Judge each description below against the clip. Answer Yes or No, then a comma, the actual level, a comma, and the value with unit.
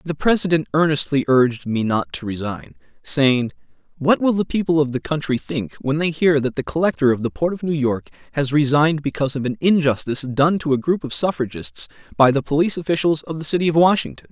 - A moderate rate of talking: No, fast, 210 wpm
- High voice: No, medium, 150 Hz